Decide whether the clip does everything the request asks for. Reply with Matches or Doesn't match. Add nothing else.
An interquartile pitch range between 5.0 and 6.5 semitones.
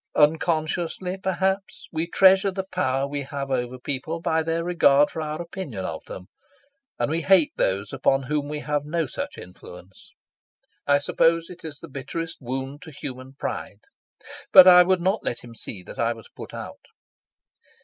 Doesn't match